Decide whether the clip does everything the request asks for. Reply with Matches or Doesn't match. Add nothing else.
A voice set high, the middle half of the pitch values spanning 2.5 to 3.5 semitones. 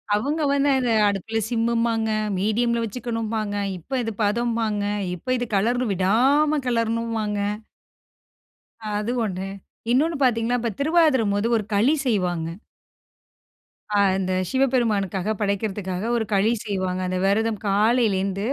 Matches